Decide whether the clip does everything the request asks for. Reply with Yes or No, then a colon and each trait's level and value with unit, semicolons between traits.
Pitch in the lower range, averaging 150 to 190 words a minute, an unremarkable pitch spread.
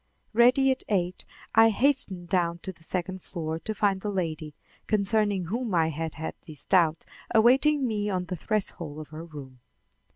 No: medium, 185 Hz; average, 170 wpm; average, 5.0 semitones